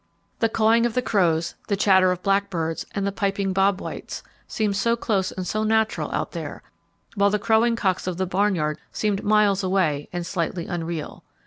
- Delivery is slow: No, average, 185 wpm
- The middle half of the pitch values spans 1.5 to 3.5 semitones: Yes, average, 2.7 semitones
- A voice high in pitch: Yes, high, 195 Hz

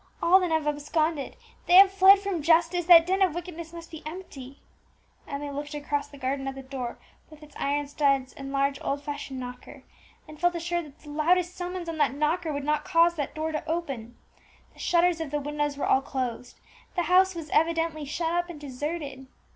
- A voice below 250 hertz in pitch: No, very high, 305 Hz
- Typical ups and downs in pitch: Yes, average, 3.3 semitones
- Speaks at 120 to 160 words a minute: No, fast, 205 wpm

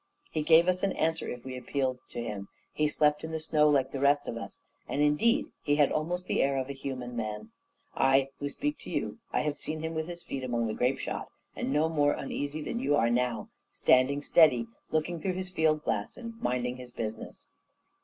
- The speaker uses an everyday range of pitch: Yes, average, 3.9 semitones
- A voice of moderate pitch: Yes, medium, 145 Hz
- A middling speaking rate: No, fast, 220 wpm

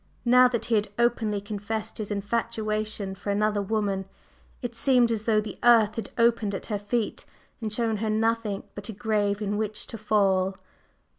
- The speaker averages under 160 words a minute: No, average, 175 wpm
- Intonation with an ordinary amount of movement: No, narrow, 2.0 semitones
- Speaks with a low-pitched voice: No, high, 215 Hz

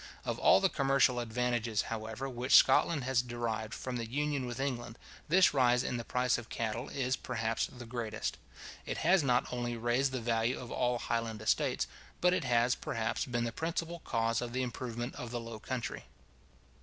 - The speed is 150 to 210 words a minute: Yes, average, 185 wpm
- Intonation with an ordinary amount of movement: No, narrow, 2.0 semitones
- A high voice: No, low, 120 Hz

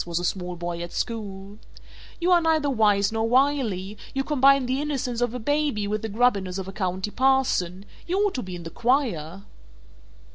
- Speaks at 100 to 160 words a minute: No, average, 190 wpm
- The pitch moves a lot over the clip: Yes, wide, 6.1 semitones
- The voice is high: Yes, high, 220 Hz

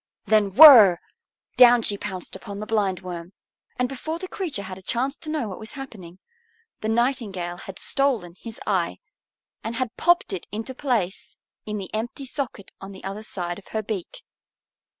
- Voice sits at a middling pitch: No, high, 215 Hz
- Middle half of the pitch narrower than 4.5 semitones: No, average, 4.8 semitones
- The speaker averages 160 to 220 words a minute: Yes, average, 170 wpm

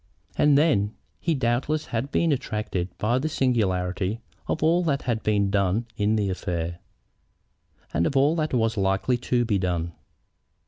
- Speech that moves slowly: No, average, 155 wpm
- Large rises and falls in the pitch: Yes, wide, 5.9 semitones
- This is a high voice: No, low, 110 Hz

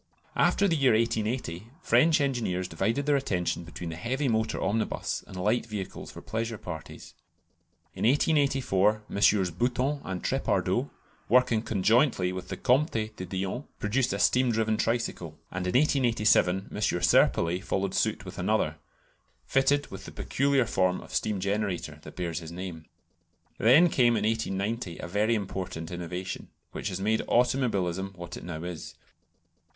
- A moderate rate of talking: Yes, average, 150 wpm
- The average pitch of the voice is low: Yes, low, 105 Hz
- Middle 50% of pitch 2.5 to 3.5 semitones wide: No, average, 5.0 semitones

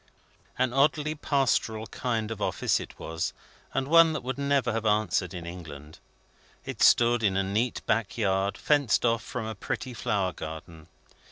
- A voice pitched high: No, low, 110 Hz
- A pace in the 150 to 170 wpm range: Yes, average, 165 wpm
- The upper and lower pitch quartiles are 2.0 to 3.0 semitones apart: No, average, 5.1 semitones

